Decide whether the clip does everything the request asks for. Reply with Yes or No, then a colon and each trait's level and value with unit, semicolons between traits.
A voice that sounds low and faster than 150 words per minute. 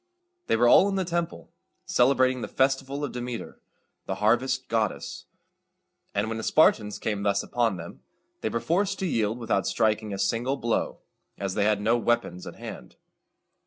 Yes: low, 120 Hz; average, 170 wpm